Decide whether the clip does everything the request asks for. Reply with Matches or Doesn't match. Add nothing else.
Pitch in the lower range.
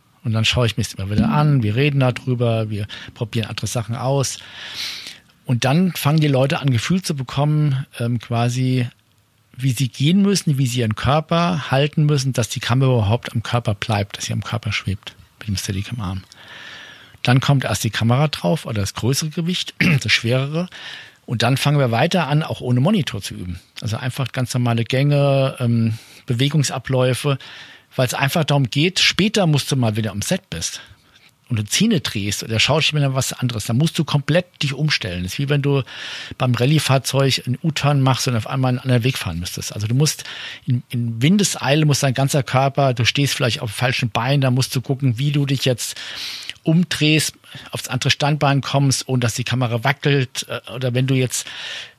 Matches